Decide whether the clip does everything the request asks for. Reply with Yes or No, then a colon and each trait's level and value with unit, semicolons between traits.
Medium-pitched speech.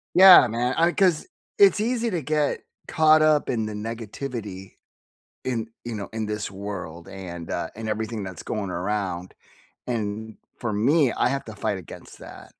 No: low, 110 Hz